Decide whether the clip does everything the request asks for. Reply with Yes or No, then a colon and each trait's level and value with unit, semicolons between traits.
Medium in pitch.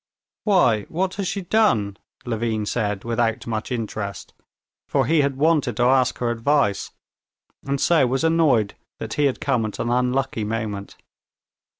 No: low, 125 Hz